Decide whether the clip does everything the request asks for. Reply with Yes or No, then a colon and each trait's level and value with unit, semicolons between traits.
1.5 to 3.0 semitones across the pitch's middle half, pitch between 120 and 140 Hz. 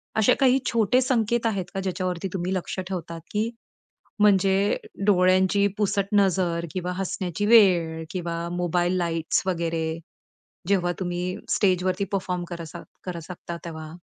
No: narrow, 2.5 semitones; medium, 185 Hz